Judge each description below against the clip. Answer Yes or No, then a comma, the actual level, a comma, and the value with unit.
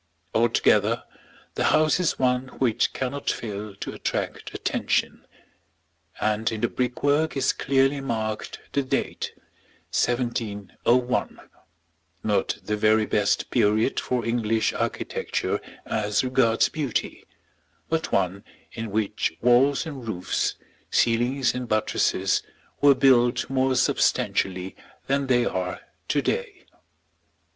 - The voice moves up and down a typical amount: Yes, average, 3.6 semitones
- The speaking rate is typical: No, slow, 110 wpm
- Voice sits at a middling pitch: No, low, 120 Hz